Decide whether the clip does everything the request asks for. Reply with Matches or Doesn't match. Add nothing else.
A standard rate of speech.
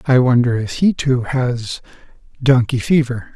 Matches